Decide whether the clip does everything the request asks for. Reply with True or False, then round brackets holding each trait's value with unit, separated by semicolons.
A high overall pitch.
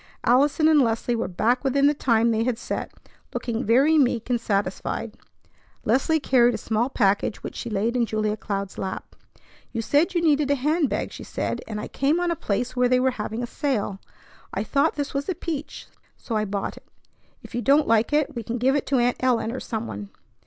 True (245 Hz)